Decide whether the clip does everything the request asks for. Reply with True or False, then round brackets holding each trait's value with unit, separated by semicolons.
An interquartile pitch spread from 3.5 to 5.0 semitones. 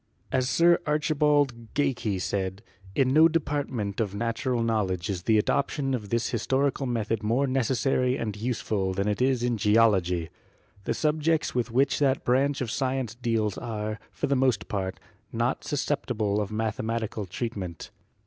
True (4.2 semitones)